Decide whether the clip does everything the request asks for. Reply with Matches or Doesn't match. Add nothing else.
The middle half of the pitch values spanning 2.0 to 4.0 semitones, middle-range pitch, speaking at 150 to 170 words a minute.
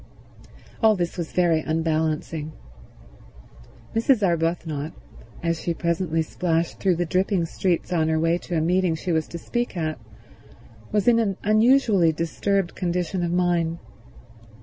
Doesn't match